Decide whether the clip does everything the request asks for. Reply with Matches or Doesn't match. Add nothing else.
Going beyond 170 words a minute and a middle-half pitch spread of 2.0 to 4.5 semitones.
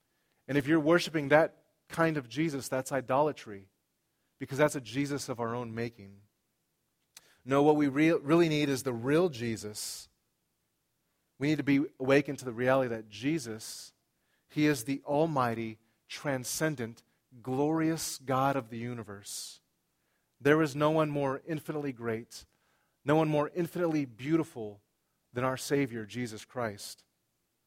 Doesn't match